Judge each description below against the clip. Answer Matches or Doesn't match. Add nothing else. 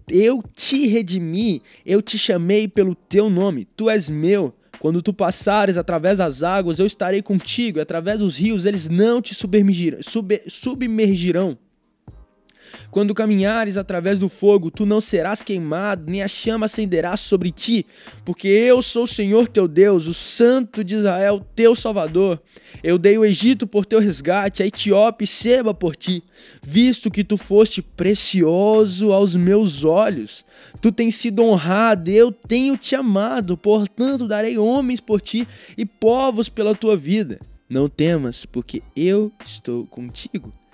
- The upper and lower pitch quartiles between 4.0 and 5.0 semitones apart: Doesn't match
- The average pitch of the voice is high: Matches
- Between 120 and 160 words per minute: Matches